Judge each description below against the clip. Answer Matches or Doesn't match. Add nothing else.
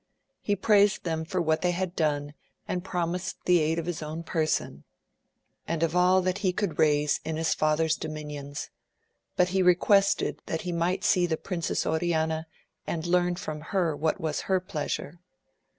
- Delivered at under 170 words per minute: Doesn't match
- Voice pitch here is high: Doesn't match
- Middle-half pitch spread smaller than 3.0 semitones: Matches